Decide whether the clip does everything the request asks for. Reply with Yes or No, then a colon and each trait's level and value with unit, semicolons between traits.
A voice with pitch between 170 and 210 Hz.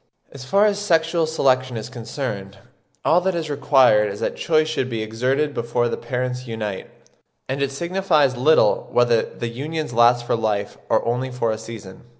No: low, 125 Hz